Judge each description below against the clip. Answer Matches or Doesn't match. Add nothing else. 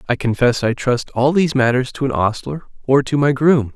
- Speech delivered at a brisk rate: Matches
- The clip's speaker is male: Matches